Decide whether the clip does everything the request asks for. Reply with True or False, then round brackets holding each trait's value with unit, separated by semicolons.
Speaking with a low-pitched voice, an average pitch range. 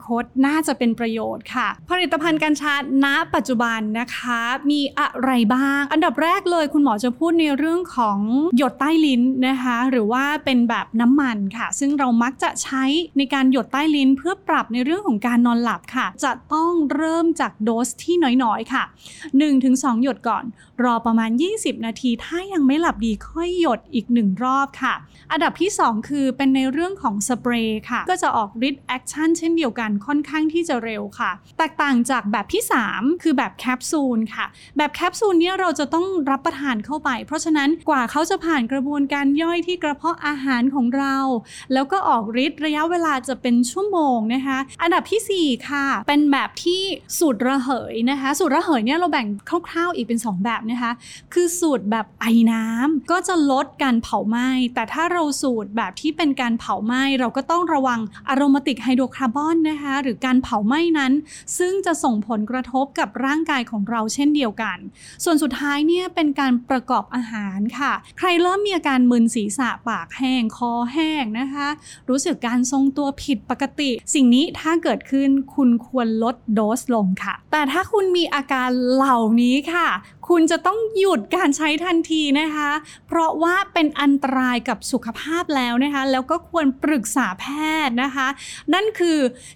False (275 Hz; 4.6 semitones)